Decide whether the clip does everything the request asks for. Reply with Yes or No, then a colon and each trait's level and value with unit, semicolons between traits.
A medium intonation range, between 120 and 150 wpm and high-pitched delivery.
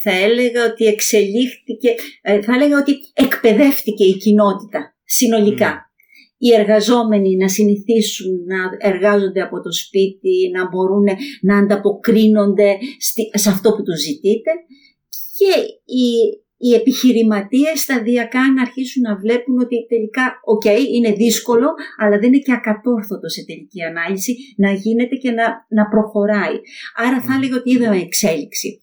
Yes: average, 3.7 semitones; average, 130 wpm; high, 225 Hz